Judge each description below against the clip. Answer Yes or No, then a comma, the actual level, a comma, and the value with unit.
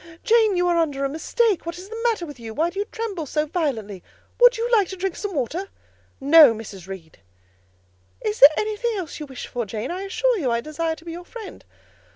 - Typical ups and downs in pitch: No, wide, 6.9 semitones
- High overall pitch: Yes, very high, 335 Hz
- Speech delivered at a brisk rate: Yes, fast, 220 wpm